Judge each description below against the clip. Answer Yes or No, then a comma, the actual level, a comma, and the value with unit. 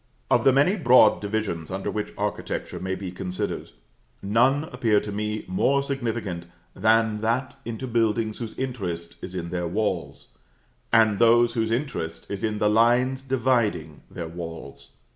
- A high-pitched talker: No, low, 110 Hz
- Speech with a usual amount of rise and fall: Yes, average, 4.4 semitones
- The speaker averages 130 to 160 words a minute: Yes, average, 150 wpm